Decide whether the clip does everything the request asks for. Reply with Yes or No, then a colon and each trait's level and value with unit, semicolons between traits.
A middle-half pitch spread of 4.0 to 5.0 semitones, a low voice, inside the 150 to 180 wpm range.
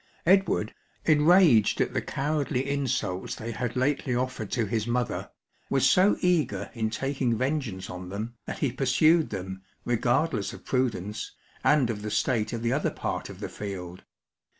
Yes: average, 4.7 semitones; low, 125 Hz; average, 160 wpm